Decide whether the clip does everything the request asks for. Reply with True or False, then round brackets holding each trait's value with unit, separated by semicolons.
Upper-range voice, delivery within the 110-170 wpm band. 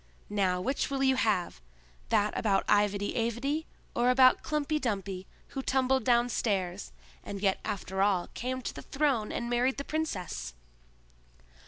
True (235 Hz; 140 wpm)